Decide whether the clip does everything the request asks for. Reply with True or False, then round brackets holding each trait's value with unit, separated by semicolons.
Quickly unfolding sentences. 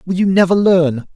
True (210 wpm)